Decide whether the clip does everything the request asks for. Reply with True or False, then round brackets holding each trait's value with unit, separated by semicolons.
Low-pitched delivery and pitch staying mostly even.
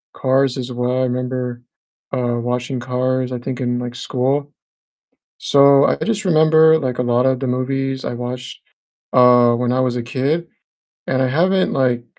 True (130 Hz; 1.8 semitones)